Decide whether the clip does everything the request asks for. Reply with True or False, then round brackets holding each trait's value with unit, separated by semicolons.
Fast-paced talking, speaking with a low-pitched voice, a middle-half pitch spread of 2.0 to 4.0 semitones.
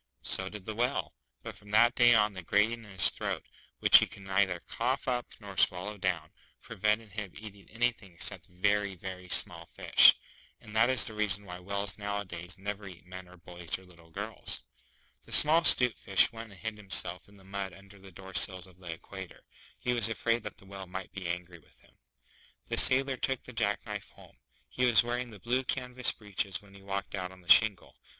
True (210 wpm; 100 Hz; 3.2 semitones)